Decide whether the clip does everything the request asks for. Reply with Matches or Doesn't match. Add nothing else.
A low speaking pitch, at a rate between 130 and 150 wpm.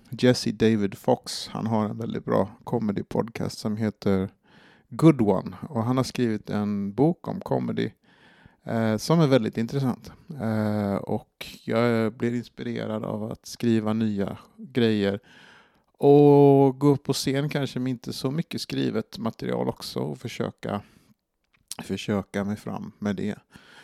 Matches